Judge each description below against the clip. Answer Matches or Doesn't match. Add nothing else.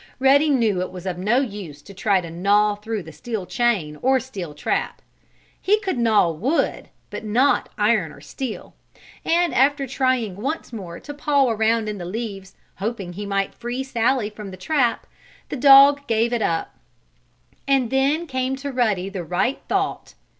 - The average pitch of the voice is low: Doesn't match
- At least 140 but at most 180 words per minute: Matches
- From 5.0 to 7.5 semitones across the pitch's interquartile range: Matches